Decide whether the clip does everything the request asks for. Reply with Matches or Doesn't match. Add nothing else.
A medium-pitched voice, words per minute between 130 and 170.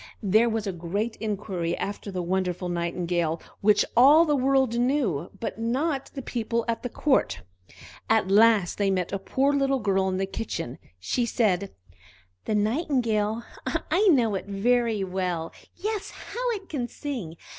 Doesn't match